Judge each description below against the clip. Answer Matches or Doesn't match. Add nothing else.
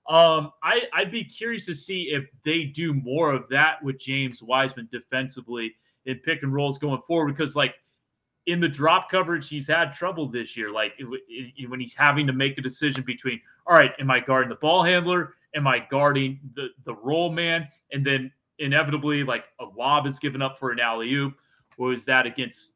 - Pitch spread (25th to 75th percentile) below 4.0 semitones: Matches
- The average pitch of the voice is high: Doesn't match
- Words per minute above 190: Matches